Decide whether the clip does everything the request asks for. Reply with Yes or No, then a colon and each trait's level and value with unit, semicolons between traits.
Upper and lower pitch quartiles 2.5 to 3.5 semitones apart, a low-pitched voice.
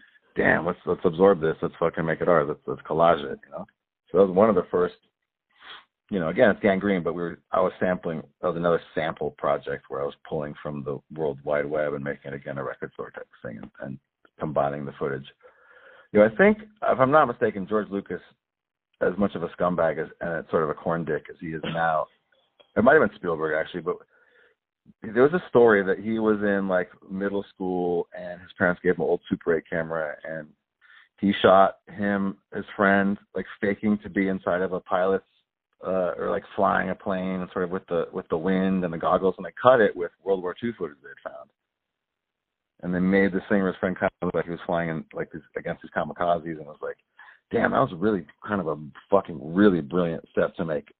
Yes: average, 2.9 semitones; very low, 95 Hz